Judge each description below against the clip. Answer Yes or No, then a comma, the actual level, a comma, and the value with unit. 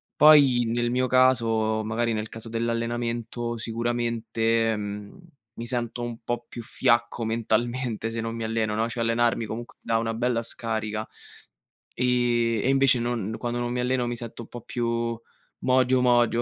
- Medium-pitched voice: No, low, 115 Hz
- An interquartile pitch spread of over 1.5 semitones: No, narrow, 1.2 semitones